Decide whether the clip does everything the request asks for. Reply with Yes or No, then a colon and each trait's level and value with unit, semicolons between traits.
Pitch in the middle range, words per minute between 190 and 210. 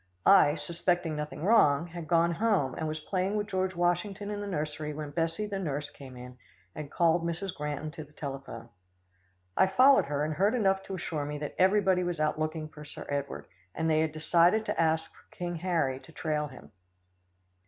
Yes: medium, 160 Hz; average, 195 wpm